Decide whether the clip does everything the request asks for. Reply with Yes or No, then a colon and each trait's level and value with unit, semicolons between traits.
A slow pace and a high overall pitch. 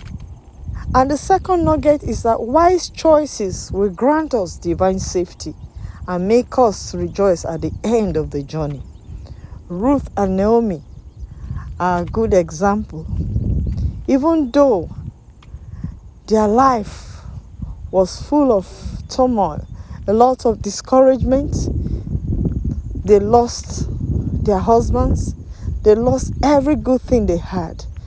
Yes: slow, 115 wpm; high, 200 Hz